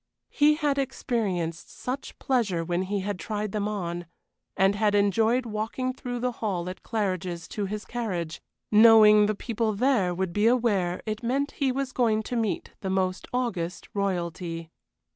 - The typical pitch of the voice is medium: No, high, 210 Hz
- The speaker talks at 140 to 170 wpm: Yes, average, 160 wpm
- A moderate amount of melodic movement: Yes, average, 4.5 semitones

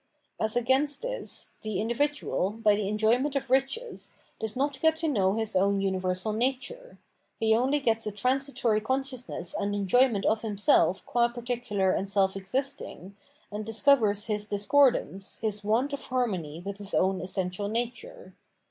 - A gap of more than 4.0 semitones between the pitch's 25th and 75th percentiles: Yes, average, 4.8 semitones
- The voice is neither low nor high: No, high, 220 Hz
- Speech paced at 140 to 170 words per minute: Yes, average, 150 wpm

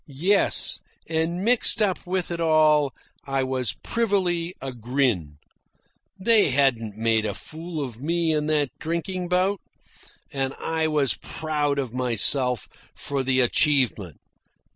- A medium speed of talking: No, slow, 130 wpm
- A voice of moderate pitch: Yes, medium, 150 Hz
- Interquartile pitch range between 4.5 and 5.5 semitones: Yes, average, 4.8 semitones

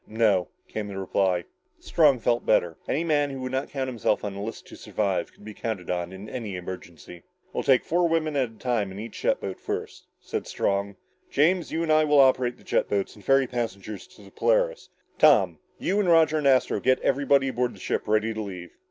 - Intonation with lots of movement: Yes, wide, 5.9 semitones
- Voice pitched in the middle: No, low, 115 Hz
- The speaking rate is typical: No, fast, 220 wpm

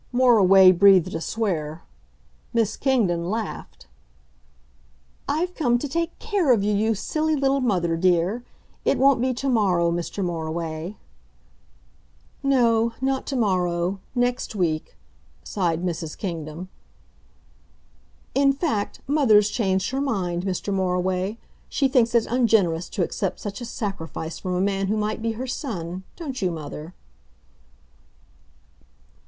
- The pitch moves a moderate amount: No, wide, 5.8 semitones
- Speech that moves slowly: Yes, slow, 130 wpm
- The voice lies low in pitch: No, high, 200 Hz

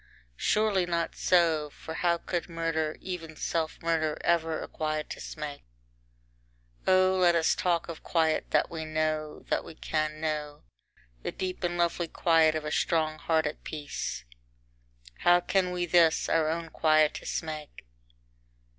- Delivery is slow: No, average, 150 wpm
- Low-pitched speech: No, medium, 160 Hz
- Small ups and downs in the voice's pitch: Yes, narrow, 1.8 semitones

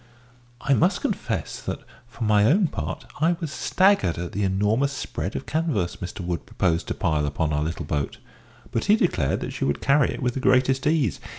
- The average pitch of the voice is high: No, low, 115 Hz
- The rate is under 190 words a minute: No, average, 200 wpm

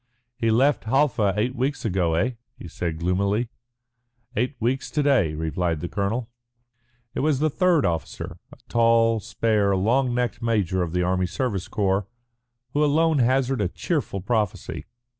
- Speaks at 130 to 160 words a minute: Yes, average, 155 wpm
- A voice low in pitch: Yes, low, 115 Hz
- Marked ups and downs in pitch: Yes, wide, 5.8 semitones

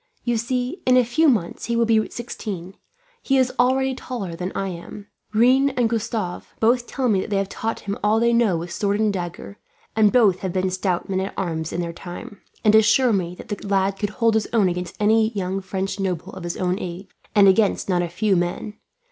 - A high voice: Yes, high, 205 Hz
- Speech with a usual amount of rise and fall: Yes, average, 3.9 semitones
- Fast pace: Yes, fast, 225 wpm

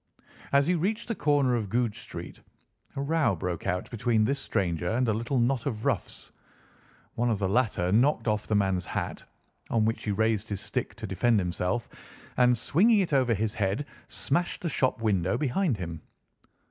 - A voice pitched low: Yes, low, 115 Hz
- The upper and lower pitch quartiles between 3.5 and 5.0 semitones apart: No, wide, 5.4 semitones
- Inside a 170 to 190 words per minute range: Yes, average, 185 wpm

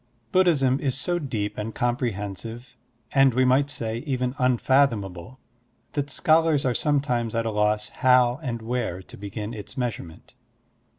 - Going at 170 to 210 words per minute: No, average, 155 wpm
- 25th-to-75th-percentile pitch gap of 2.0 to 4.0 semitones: Yes, average, 3.5 semitones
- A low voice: Yes, low, 125 Hz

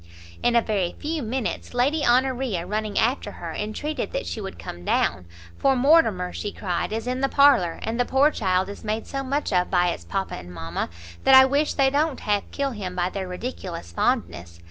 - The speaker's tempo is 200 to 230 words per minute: Yes, fast, 205 wpm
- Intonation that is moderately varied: No, wide, 6.7 semitones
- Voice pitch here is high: Yes, high, 220 Hz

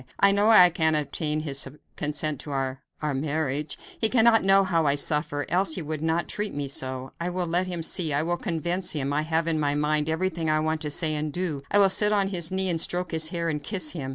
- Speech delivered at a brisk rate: Yes, fast, 245 wpm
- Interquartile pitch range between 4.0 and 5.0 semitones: No, average, 3.2 semitones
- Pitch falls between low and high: Yes, medium, 160 Hz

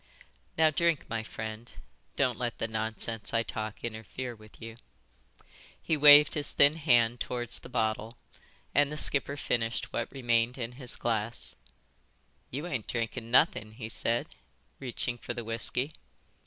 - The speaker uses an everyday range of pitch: Yes, average, 3.1 semitones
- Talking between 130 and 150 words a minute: Yes, average, 145 wpm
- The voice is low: Yes, low, 120 Hz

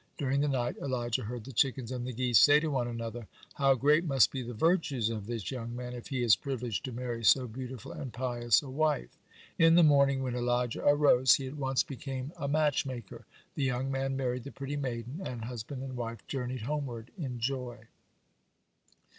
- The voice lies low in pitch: Yes, low, 130 Hz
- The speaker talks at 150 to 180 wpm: No, average, 195 wpm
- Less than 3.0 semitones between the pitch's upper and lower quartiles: Yes, narrow, 2.4 semitones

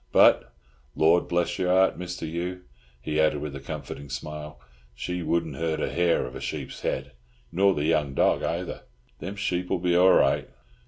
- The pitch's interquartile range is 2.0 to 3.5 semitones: Yes, average, 2.9 semitones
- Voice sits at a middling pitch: No, very low, 85 Hz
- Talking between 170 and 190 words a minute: Yes, average, 175 wpm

